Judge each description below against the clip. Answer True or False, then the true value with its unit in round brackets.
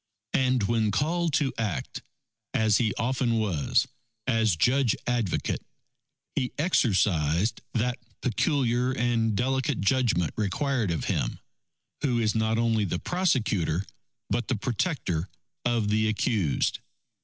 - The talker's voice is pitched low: True (115 Hz)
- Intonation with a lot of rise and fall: False (3.7 semitones)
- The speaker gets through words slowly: True (120 wpm)